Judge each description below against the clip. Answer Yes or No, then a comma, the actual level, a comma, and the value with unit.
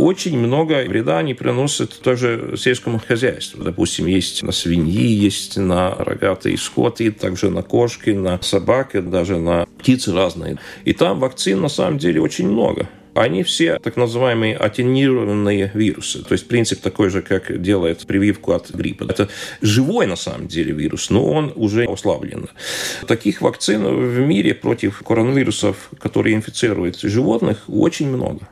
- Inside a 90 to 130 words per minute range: No, average, 145 wpm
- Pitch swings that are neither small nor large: Yes, average, 4.5 semitones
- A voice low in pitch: Yes, low, 110 Hz